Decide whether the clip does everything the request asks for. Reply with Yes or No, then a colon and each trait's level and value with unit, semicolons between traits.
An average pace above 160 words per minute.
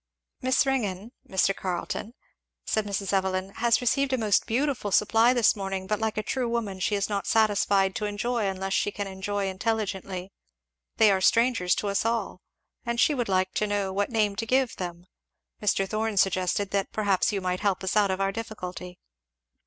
Yes: average, 185 wpm